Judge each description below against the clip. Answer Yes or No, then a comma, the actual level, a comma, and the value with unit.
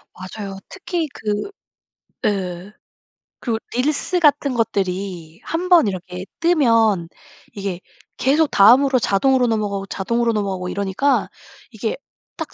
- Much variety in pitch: Yes, wide, 6.0 semitones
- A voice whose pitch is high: Yes, high, 210 Hz